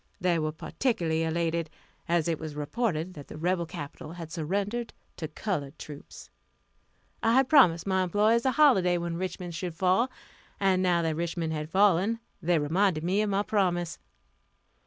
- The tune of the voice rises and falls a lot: No, average, 3.6 semitones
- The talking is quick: No, average, 160 wpm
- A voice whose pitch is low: No, medium, 175 Hz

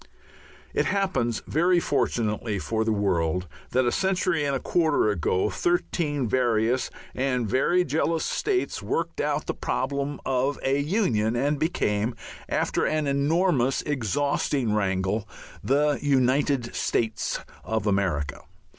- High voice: No, low, 130 Hz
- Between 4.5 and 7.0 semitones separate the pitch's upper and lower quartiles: Yes, average, 5.2 semitones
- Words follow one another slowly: Yes, slow, 125 wpm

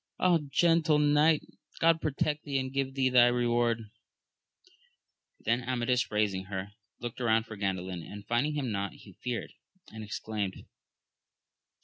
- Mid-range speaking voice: No, low, 120 Hz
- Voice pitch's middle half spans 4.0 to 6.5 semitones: Yes, average, 4.8 semitones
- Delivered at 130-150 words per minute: Yes, average, 140 wpm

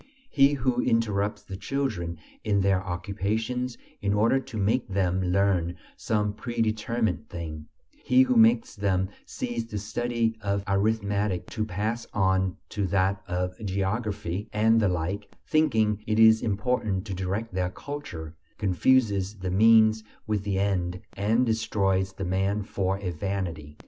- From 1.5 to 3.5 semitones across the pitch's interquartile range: Yes, average, 2.9 semitones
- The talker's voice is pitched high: No, low, 100 Hz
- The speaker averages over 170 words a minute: No, average, 145 wpm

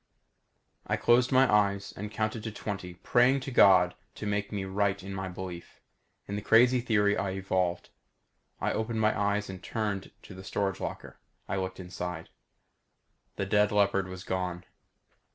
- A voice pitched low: Yes, low, 100 Hz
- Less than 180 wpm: Yes, average, 165 wpm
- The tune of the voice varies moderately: No, narrow, 2.3 semitones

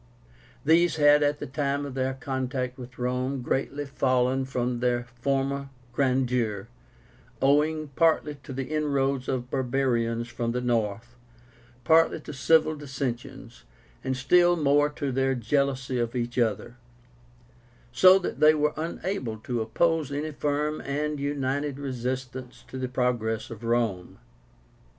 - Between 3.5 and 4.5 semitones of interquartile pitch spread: No, average, 2.9 semitones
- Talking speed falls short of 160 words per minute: Yes, slow, 135 wpm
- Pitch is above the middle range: No, low, 135 Hz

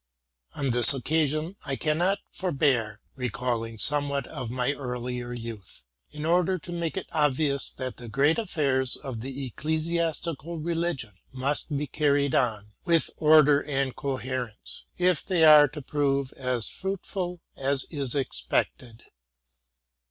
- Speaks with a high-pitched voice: No, medium, 140 Hz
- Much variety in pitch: No, average, 3.9 semitones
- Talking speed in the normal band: No, slow, 130 wpm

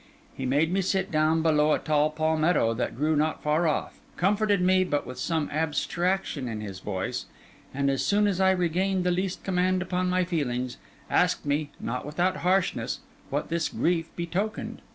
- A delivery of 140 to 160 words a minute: No, average, 175 wpm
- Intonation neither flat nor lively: Yes, average, 3.9 semitones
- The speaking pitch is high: No, medium, 165 Hz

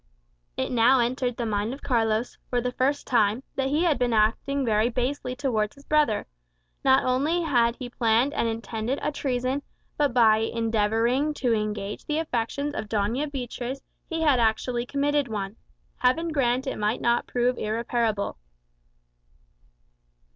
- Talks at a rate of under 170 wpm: Yes, average, 155 wpm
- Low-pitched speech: No, high, 245 Hz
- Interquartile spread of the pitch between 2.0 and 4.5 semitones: Yes, average, 3.5 semitones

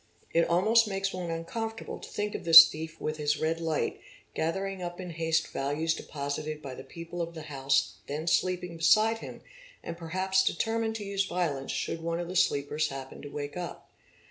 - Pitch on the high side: No, medium, 165 Hz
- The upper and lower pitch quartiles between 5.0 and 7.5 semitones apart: No, average, 3.5 semitones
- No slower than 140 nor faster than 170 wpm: No, average, 195 wpm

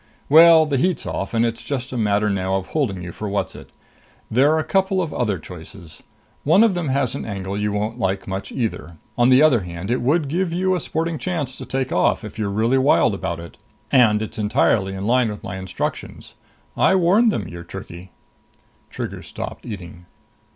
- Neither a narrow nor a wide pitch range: No, wide, 7.5 semitones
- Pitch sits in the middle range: No, low, 115 Hz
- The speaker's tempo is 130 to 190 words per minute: No, average, 200 wpm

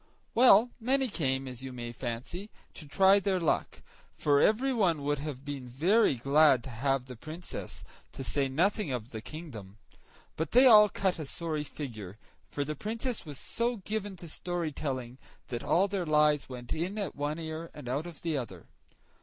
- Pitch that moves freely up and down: Yes, wide, 6.4 semitones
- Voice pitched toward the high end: No, medium, 150 Hz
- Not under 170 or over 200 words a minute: Yes, average, 180 wpm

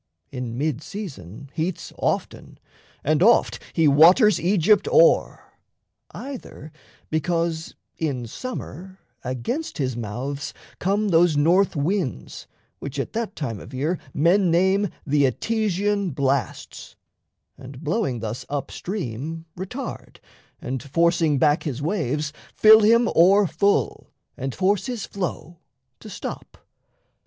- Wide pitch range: Yes, wide, 6.1 semitones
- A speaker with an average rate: No, slow, 110 wpm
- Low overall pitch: No, medium, 165 Hz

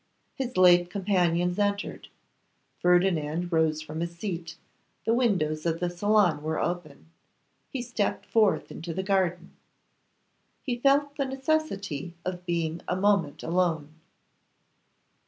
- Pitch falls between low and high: Yes, medium, 180 Hz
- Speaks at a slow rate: Yes, slow, 120 wpm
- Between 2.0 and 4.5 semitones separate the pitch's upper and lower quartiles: Yes, average, 3.7 semitones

